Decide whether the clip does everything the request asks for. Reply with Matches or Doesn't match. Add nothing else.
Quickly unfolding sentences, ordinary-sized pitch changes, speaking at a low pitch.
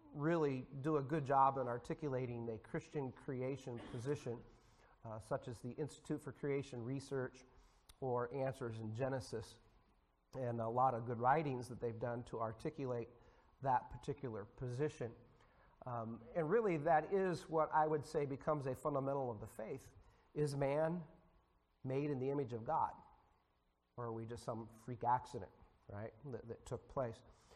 Doesn't match